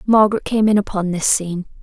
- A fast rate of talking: No, average, 195 wpm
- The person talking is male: No, female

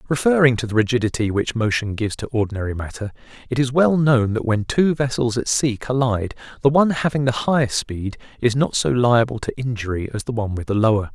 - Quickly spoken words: Yes, fast, 210 wpm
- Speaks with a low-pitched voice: Yes, low, 120 Hz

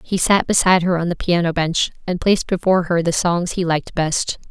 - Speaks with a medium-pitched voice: Yes, medium, 175 Hz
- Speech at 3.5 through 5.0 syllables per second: No, 5.8 syllables/s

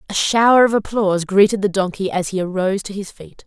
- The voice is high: Yes, high, 195 Hz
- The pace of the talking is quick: Yes, fast, 225 wpm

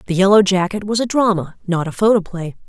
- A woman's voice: Yes, female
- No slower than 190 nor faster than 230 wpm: Yes, average, 200 wpm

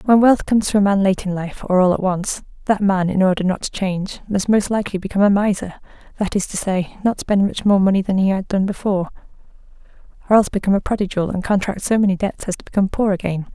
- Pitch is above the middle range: Yes, high, 195 Hz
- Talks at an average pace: No, fast, 240 wpm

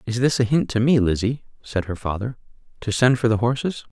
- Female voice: No, male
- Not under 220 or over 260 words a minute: Yes, fast, 225 wpm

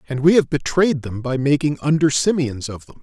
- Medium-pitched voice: Yes, medium, 145 Hz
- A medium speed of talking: No, fast, 220 wpm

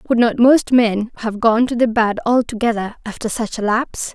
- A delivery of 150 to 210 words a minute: Yes, fast, 205 wpm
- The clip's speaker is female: Yes, female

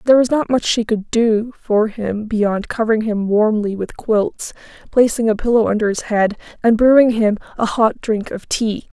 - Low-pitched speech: No, high, 220 Hz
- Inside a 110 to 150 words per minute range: No, average, 195 wpm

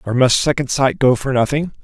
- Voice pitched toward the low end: Yes, low, 130 Hz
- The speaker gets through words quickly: Yes, fast, 230 wpm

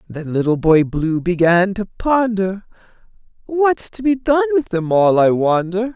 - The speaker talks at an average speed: Yes, average, 160 wpm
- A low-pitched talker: No, high, 200 Hz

